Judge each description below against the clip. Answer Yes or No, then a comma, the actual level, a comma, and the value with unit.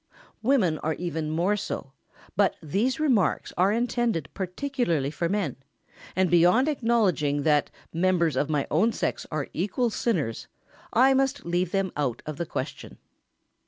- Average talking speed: Yes, average, 145 wpm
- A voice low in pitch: No, medium, 180 Hz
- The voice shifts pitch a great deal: Yes, wide, 6.9 semitones